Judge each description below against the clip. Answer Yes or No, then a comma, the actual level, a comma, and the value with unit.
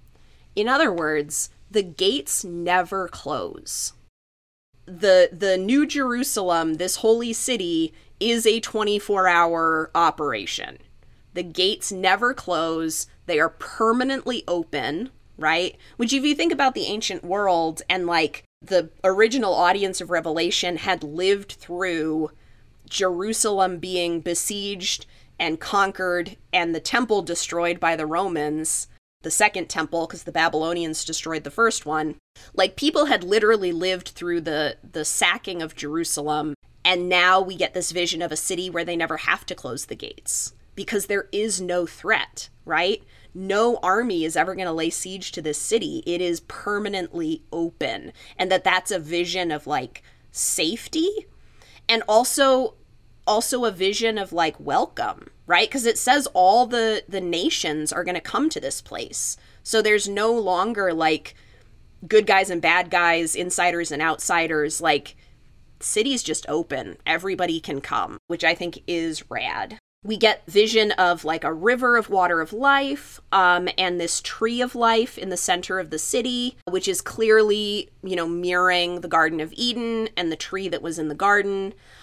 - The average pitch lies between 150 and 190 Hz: Yes, medium, 185 Hz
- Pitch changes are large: No, average, 4.8 semitones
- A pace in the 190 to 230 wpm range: No, average, 155 wpm